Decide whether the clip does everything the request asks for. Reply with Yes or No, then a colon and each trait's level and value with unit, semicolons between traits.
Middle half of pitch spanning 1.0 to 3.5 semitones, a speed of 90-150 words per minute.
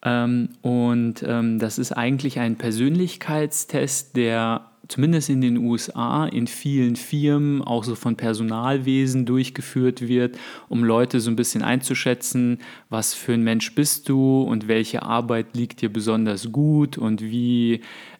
Yes: narrow, 2.5 semitones; average, 140 wpm